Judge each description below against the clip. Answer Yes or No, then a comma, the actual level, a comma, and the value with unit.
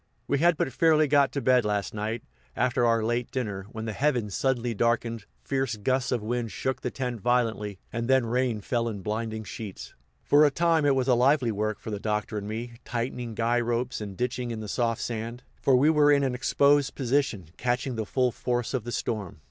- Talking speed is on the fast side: Yes, fast, 210 wpm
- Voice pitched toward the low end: Yes, low, 120 Hz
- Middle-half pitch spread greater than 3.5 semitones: No, average, 3.0 semitones